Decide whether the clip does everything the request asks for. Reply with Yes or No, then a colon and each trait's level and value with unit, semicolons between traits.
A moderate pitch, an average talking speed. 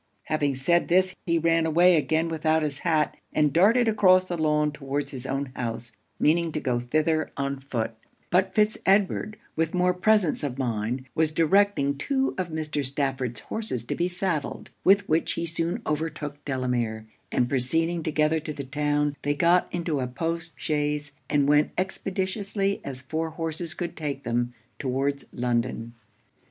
Yes: medium, 155 Hz; average, 165 wpm